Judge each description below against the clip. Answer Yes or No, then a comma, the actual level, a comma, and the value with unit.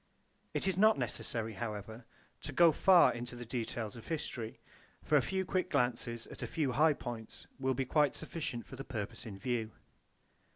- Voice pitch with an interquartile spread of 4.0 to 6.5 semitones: Yes, average, 5.1 semitones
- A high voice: No, low, 125 Hz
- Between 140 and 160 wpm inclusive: No, average, 180 wpm